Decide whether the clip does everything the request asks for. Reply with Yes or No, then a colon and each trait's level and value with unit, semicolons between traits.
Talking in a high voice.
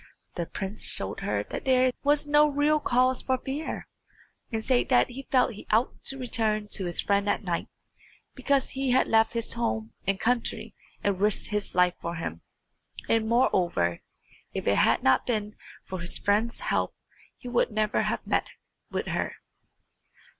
Yes: high, 225 Hz